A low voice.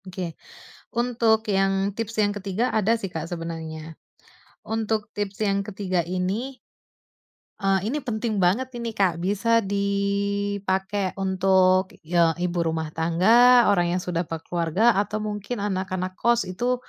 No: high, 195 Hz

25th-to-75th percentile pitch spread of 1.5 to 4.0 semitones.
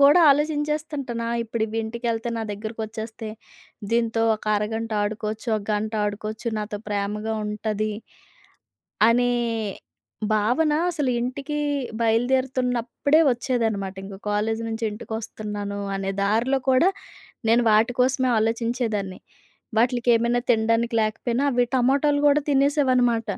Yes: average, 2.8 semitones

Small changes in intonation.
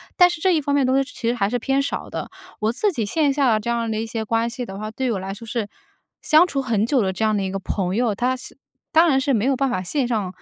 No: average, 4.2 semitones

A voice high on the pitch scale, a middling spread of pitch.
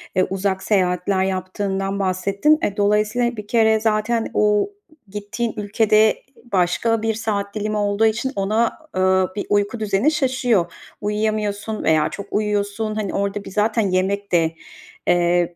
No: high, 205 Hz; narrow, 2.2 semitones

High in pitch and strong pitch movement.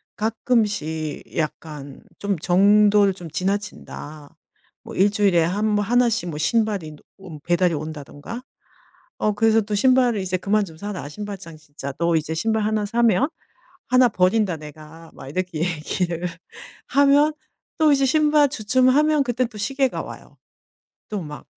Yes: high, 200 Hz; wide, 5.8 semitones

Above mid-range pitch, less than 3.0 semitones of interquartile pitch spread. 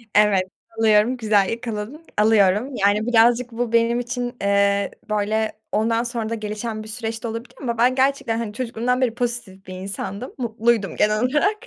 Yes: high, 225 Hz; narrow, 2.5 semitones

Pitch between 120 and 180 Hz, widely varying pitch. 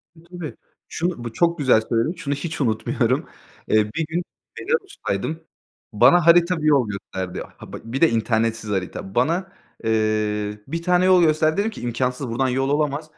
Yes: medium, 140 Hz; wide, 7.1 semitones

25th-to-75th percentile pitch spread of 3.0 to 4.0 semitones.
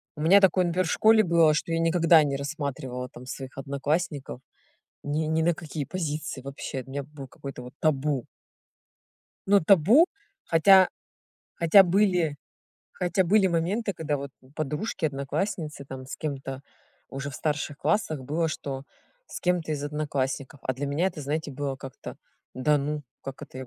Yes: average, 3.6 semitones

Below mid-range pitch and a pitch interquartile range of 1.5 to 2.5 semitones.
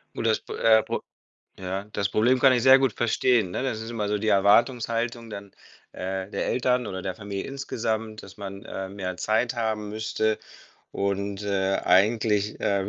No: low, 110 Hz; average, 2.9 semitones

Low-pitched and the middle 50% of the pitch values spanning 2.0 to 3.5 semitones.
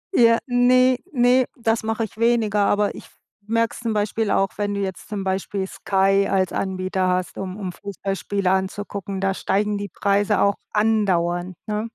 No: high, 205 Hz; narrow, 2.6 semitones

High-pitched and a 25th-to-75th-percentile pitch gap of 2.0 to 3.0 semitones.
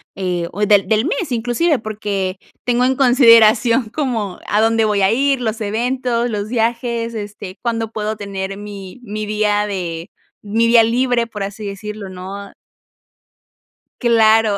Yes: high, 220 Hz; narrow, 2.6 semitones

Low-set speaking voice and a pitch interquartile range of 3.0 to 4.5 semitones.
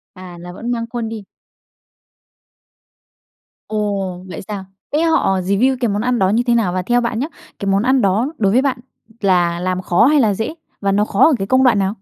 No: high, 210 Hz; average, 4.2 semitones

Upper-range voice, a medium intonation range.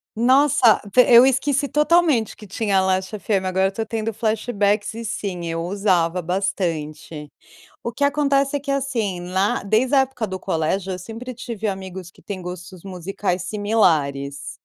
Yes: high, 200 Hz; average, 4.6 semitones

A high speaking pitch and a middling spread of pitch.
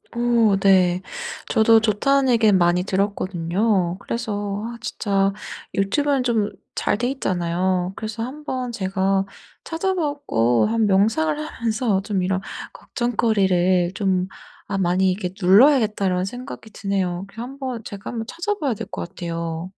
Yes: high, 200 Hz; average, 4.2 semitones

